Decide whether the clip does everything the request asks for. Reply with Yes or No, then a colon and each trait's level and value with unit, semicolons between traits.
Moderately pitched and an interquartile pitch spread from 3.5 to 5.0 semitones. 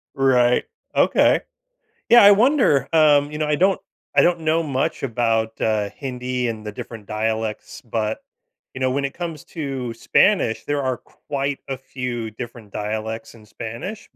No: low, 130 Hz; average, 4.7 semitones